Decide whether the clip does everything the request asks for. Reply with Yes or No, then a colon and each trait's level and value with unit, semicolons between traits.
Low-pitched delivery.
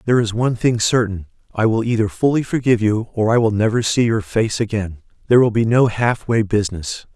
Yes: low, 110 Hz